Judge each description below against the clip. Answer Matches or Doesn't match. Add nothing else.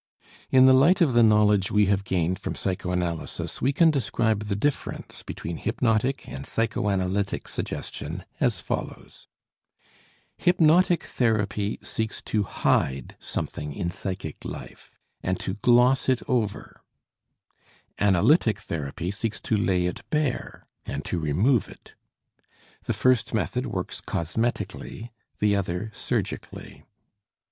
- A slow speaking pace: Matches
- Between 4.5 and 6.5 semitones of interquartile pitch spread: Matches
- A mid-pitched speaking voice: Doesn't match